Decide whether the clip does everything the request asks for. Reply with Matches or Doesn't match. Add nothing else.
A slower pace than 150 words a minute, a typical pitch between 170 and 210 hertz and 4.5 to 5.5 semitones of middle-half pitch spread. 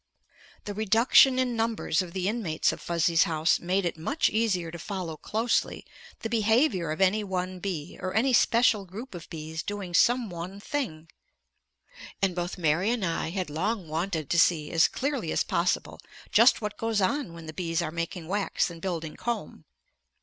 Doesn't match